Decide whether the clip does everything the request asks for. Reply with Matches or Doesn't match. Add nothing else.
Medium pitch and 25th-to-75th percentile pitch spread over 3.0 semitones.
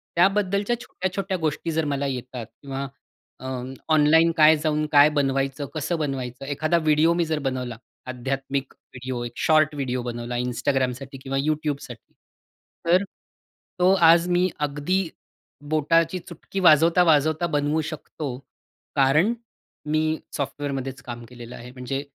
Matches